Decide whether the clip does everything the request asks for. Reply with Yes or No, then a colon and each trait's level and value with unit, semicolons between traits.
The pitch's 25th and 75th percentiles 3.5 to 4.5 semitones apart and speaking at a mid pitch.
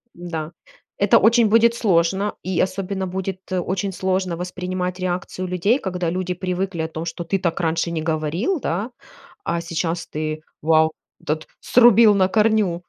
No: narrow, 2.6 semitones; medium, 180 Hz